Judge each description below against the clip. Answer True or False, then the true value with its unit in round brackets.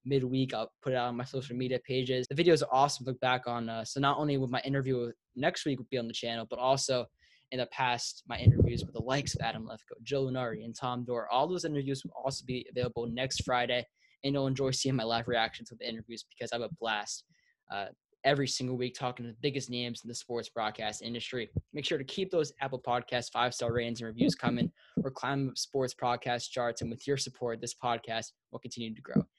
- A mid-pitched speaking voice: False (125 Hz)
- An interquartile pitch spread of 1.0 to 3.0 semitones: True (2.4 semitones)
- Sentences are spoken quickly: True (240 wpm)